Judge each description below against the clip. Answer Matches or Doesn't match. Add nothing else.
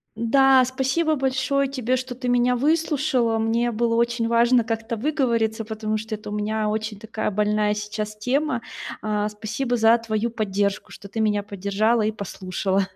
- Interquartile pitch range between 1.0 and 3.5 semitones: Matches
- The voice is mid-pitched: Doesn't match